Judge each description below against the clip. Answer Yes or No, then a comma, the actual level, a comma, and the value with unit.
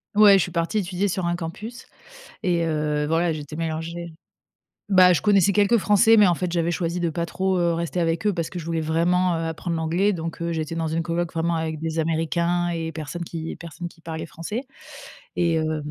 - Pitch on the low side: No, medium, 170 Hz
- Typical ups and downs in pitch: No, narrow, 1.8 semitones